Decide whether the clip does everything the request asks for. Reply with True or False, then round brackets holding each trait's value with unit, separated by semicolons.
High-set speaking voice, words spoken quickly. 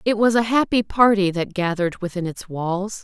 False (200 Hz; 195 wpm)